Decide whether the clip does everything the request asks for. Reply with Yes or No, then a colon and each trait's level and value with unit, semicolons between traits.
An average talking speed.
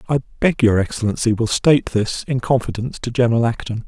Yes: average, 185 wpm